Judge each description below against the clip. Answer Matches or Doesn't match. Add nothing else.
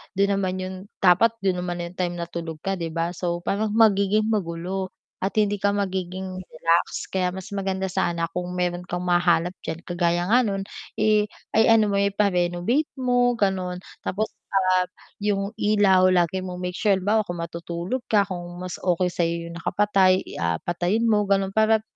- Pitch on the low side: Doesn't match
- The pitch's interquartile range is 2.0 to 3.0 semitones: Matches